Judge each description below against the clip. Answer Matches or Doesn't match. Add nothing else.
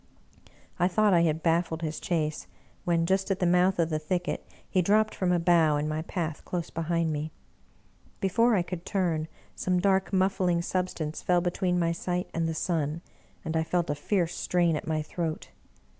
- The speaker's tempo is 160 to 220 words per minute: Matches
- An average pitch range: Doesn't match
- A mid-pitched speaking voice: Matches